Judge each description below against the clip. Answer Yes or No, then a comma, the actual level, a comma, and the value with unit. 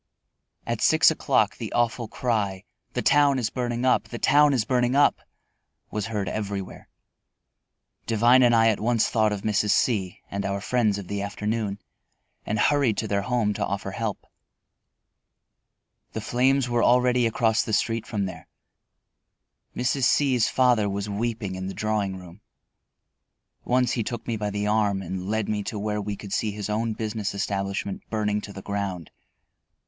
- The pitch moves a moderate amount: Yes, average, 3.0 semitones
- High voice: No, low, 110 Hz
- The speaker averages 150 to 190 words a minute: Yes, average, 170 wpm